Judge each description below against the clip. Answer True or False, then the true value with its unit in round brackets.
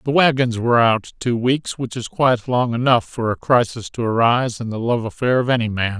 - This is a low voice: True (120 Hz)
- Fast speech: True (220 wpm)